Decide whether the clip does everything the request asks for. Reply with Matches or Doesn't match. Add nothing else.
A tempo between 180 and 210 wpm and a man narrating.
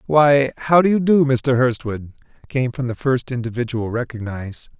Doesn't match